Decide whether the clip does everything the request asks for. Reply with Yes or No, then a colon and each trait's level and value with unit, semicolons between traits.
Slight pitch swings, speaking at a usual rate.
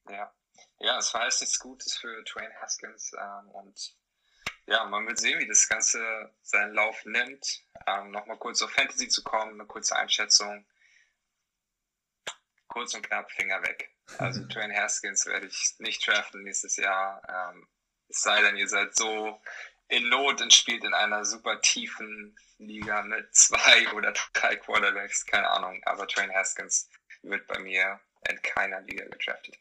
Yes: narrow, 1.3 semitones; average, 160 wpm